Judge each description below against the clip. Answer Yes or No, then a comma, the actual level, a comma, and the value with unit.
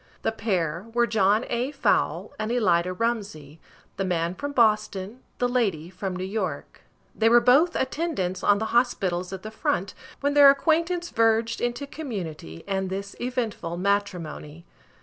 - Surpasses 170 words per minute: No, average, 150 wpm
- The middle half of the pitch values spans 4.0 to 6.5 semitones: Yes, average, 5.0 semitones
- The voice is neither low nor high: No, high, 215 Hz